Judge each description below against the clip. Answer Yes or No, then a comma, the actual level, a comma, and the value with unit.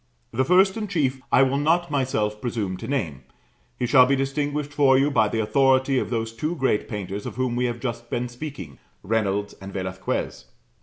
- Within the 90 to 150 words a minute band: No, average, 195 wpm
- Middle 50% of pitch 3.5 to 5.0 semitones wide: Yes, average, 4.7 semitones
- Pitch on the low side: Yes, low, 125 Hz